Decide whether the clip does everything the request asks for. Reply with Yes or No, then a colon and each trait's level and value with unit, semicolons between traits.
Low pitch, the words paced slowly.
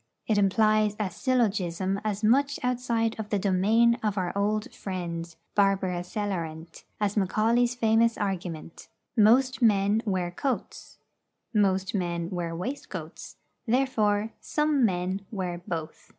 No: high, 205 Hz; slow, 120 wpm